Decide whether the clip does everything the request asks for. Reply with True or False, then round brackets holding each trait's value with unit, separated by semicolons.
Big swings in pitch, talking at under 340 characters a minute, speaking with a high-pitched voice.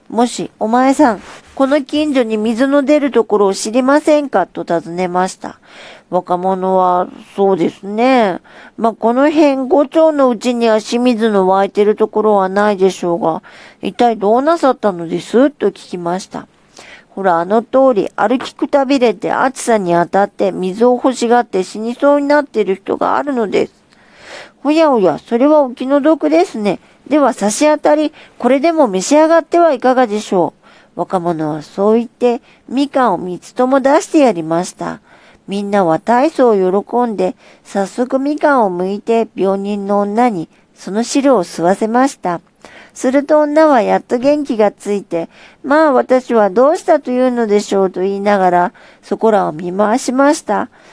True (5.9 semitones; 320 characters per minute; 230 Hz)